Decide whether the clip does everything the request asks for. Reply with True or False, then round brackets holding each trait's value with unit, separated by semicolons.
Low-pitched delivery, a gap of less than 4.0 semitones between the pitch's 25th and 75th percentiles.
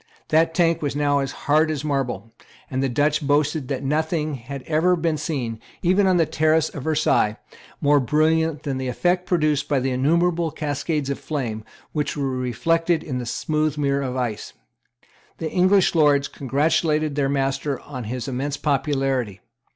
False (145 Hz; 2.8 semitones)